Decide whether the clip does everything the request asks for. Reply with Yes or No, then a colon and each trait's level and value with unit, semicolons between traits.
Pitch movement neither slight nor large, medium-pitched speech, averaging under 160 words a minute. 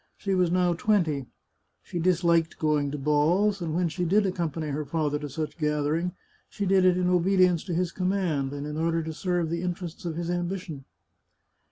No: average, 3.0 semitones; medium, 170 Hz; average, 190 wpm